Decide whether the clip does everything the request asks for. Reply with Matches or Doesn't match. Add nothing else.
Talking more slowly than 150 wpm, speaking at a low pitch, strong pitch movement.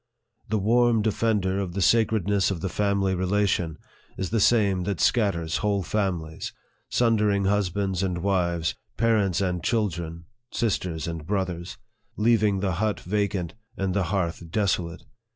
Doesn't match